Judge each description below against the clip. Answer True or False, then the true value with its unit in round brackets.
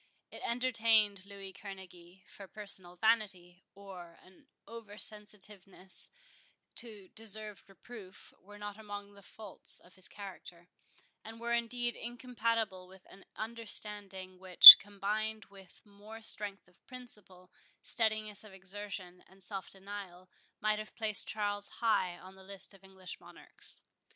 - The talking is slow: True (130 wpm)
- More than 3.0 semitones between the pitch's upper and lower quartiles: False (2.4 semitones)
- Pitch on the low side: False (205 Hz)